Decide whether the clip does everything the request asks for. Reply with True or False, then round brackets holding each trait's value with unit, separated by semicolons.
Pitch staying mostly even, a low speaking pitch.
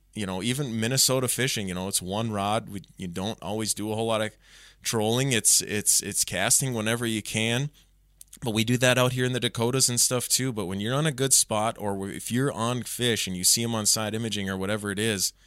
False (3.2 semitones; 110 Hz)